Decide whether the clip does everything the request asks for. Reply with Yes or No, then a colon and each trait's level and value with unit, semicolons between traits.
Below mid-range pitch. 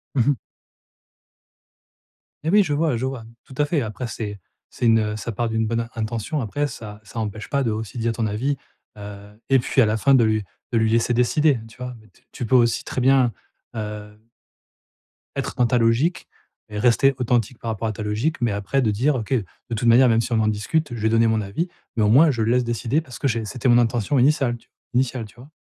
Yes: low, 115 Hz